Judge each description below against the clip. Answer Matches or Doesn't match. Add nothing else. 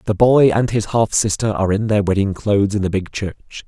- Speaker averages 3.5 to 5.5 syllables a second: Matches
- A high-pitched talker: Doesn't match